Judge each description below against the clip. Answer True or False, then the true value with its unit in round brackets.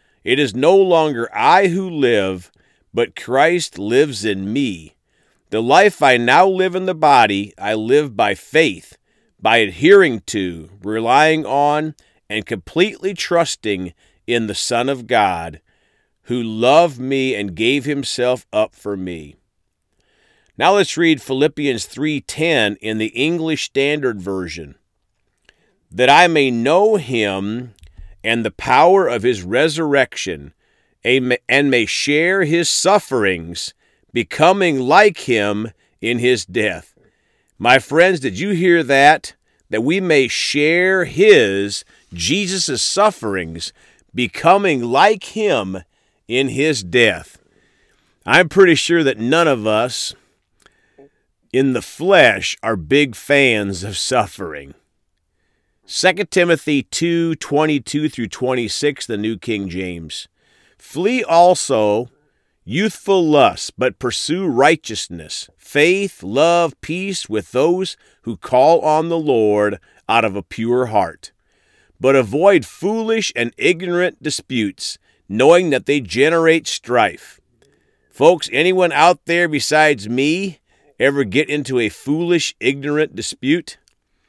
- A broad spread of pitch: True (7.9 semitones)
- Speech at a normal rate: False (120 wpm)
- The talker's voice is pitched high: False (135 Hz)